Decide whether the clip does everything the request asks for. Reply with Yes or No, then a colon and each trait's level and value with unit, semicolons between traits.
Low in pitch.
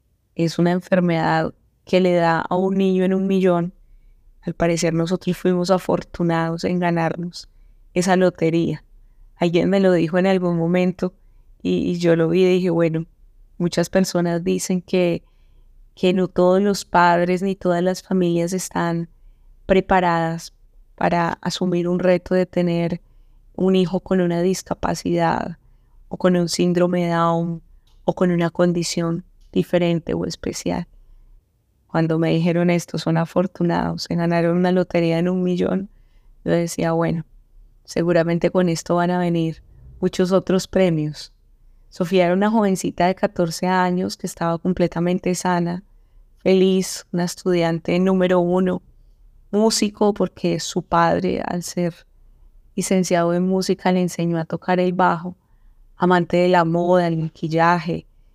No: medium, 175 Hz